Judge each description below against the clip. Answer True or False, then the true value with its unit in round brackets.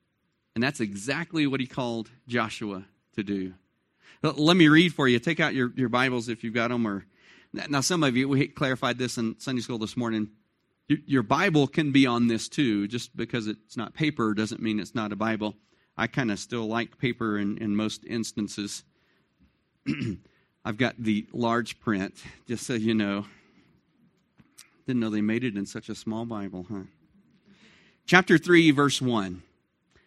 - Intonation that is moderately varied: True (3.9 semitones)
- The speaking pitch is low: True (115 Hz)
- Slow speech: False (175 wpm)